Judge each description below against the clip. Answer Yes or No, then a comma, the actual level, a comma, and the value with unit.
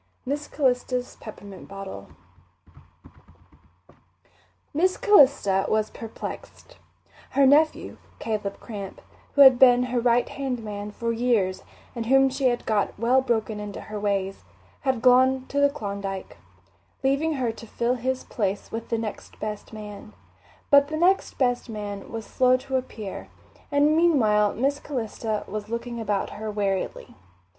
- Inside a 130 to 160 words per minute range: Yes, average, 140 wpm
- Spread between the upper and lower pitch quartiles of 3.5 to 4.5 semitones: Yes, average, 4.1 semitones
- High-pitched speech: Yes, high, 235 Hz